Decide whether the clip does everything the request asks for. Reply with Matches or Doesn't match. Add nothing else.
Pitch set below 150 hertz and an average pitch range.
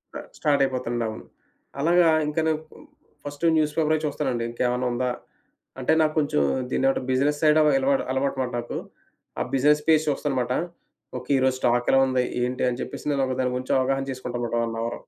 Matches